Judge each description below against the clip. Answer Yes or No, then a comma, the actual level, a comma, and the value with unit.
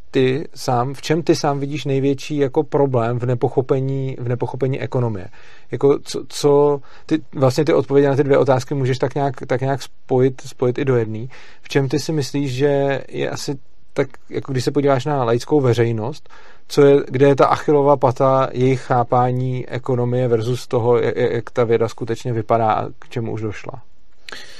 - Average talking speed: No, fast, 185 wpm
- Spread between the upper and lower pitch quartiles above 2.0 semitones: Yes, narrow, 2.5 semitones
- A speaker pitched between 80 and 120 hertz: No, low, 135 Hz